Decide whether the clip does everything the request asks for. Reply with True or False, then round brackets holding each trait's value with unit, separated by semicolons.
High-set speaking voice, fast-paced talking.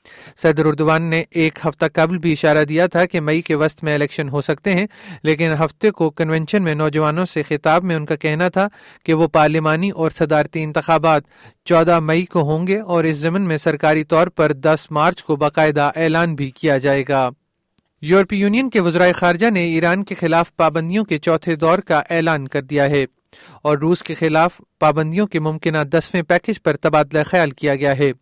False (160 Hz; 195 wpm)